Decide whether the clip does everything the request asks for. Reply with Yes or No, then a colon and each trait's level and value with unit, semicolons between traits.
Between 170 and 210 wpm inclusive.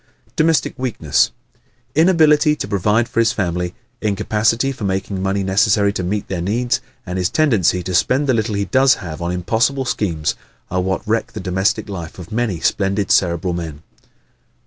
Yes: average, 175 wpm